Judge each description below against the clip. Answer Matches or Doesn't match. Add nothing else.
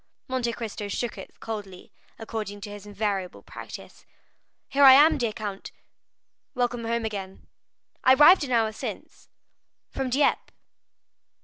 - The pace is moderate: Doesn't match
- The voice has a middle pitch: Doesn't match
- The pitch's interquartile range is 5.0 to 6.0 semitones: Doesn't match